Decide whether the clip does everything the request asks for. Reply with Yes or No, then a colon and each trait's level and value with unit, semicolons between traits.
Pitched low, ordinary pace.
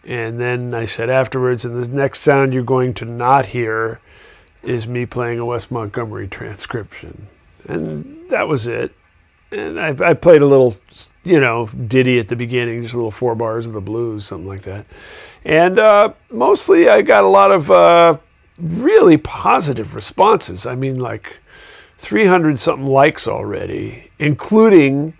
Yes: low, 125 Hz; average, 160 wpm